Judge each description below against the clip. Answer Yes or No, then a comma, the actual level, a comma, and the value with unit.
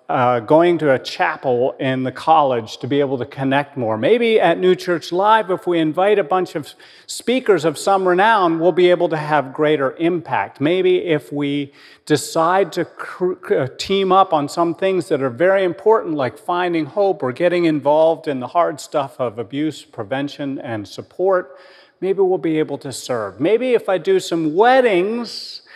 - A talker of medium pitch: Yes, medium, 170 Hz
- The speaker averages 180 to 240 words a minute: Yes, average, 185 wpm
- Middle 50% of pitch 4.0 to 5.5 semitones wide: Yes, average, 4.5 semitones